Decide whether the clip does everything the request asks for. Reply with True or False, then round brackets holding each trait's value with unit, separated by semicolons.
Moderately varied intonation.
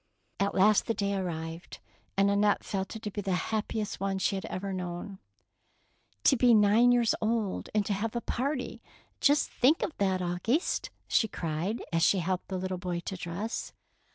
True (3.2 semitones)